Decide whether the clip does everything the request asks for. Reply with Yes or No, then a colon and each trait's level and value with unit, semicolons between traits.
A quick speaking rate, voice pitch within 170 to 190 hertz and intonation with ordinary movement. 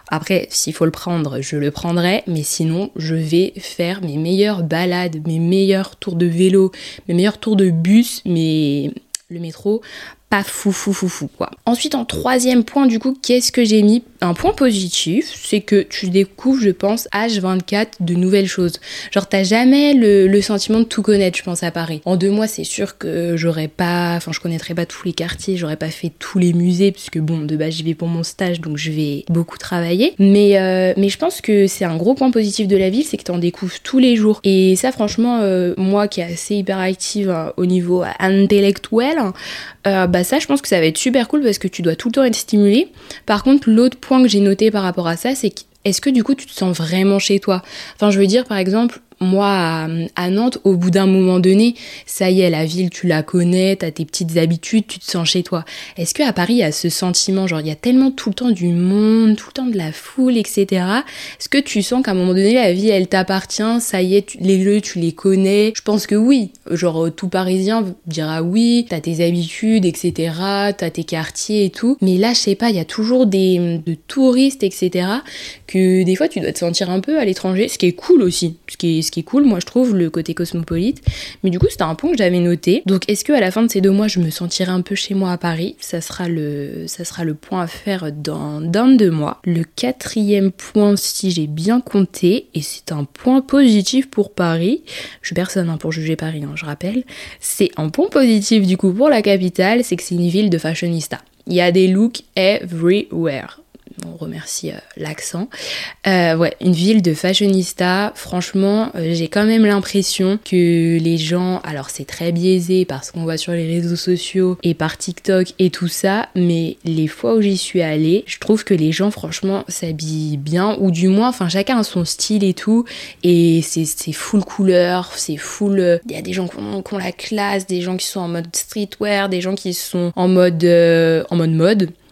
Yes: fast, 230 wpm; medium, 185 Hz; average, 3.4 semitones